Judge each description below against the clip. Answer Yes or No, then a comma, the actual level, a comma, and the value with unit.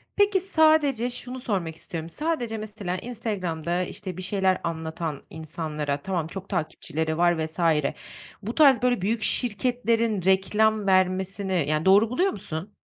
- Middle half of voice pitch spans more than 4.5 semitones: Yes, wide, 5.5 semitones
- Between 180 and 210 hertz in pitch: Yes, high, 190 Hz